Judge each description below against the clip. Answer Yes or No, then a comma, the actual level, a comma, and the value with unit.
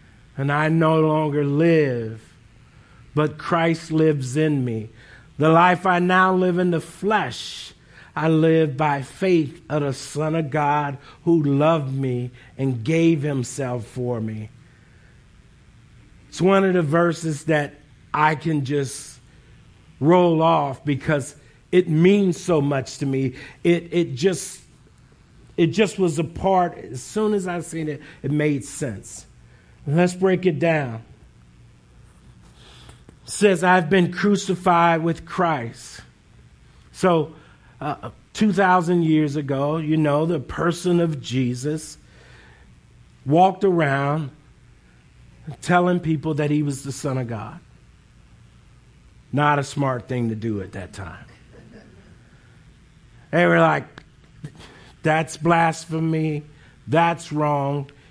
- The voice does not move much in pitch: No, average, 4.2 semitones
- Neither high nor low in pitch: Yes, medium, 150 Hz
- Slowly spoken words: Yes, slow, 125 wpm